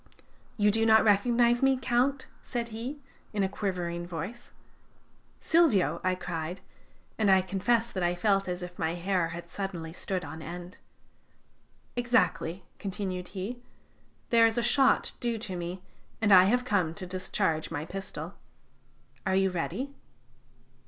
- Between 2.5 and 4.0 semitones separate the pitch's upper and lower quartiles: No, average, 4.6 semitones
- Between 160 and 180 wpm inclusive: No, average, 145 wpm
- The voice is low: No, high, 195 Hz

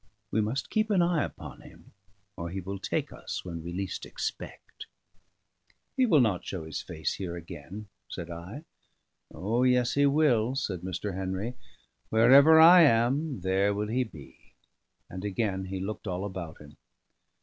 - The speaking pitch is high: No, low, 105 Hz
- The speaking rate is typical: Yes, average, 160 wpm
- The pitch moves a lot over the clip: Yes, wide, 5.7 semitones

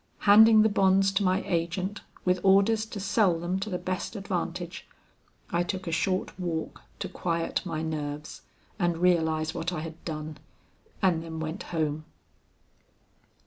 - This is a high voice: No, medium, 175 Hz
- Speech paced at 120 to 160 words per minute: Yes, average, 150 wpm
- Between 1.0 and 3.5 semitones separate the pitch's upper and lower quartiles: Yes, average, 3.1 semitones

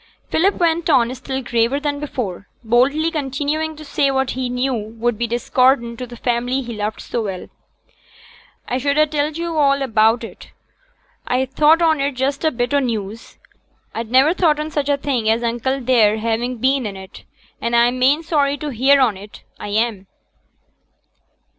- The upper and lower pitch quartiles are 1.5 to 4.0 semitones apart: Yes, average, 3.6 semitones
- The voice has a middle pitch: No, very high, 255 Hz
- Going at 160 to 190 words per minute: Yes, average, 185 wpm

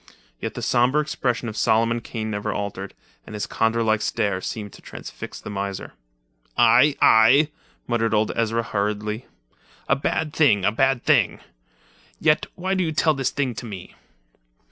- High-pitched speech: No, low, 115 Hz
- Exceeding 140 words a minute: Yes, average, 165 wpm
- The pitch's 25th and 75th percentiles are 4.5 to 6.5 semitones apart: No, average, 4.1 semitones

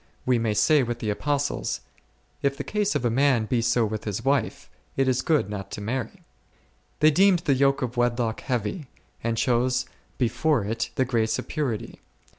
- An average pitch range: Yes, average, 3.6 semitones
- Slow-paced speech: No, average, 185 wpm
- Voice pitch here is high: No, low, 125 Hz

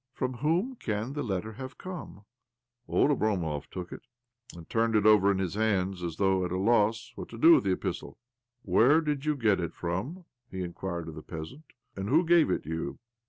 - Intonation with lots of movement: Yes, wide, 6.2 semitones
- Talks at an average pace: No, fast, 225 wpm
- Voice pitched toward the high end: No, low, 110 Hz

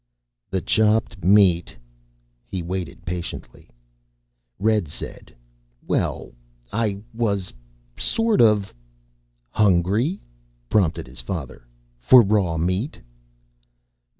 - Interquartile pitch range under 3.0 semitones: No, average, 4.3 semitones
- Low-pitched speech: Yes, very low, 95 Hz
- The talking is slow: Yes, slow, 90 wpm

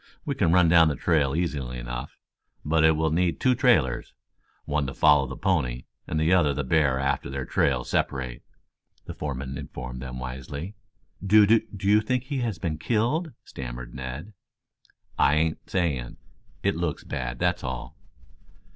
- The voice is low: Yes, very low, 75 Hz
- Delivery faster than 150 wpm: Yes, average, 165 wpm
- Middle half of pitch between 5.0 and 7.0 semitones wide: Yes, wide, 5.6 semitones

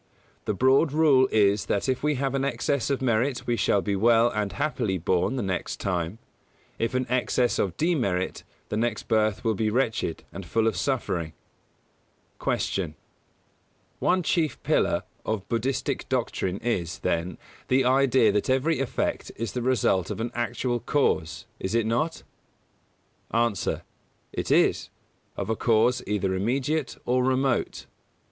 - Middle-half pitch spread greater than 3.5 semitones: Yes, average, 4.6 semitones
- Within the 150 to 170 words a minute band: Yes, average, 155 wpm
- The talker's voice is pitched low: Yes, low, 115 Hz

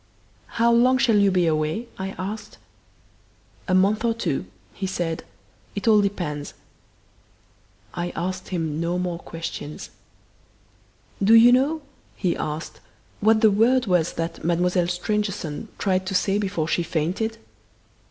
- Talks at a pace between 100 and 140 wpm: Yes, slow, 135 wpm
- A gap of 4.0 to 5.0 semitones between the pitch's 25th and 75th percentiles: Yes, average, 4.3 semitones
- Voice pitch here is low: No, medium, 185 Hz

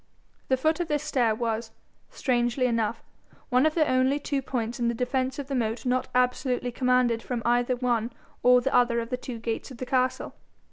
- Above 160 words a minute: Yes, average, 200 wpm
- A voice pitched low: No, very high, 250 Hz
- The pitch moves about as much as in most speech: No, narrow, 1.8 semitones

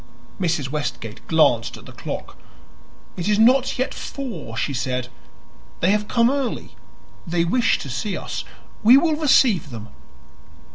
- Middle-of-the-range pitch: Yes, medium, 180 Hz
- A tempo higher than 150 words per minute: No, average, 145 wpm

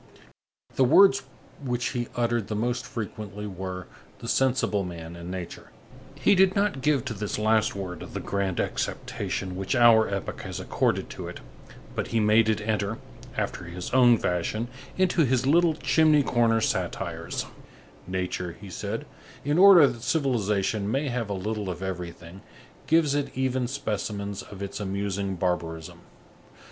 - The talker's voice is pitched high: No, low, 110 Hz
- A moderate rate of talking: Yes, average, 155 wpm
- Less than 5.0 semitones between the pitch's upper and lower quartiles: No, average, 5.3 semitones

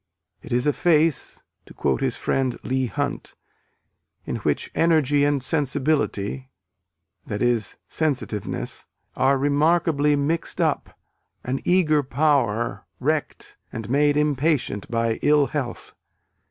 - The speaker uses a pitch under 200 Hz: Yes, medium, 140 Hz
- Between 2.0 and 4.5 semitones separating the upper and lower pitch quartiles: Yes, average, 3.1 semitones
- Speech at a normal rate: No, slow, 115 wpm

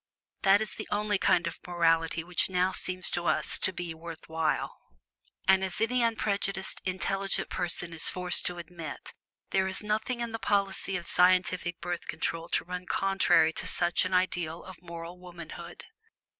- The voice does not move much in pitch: Yes, narrow, 2.2 semitones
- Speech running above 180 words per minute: No, average, 170 wpm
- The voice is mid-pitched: Yes, medium, 180 Hz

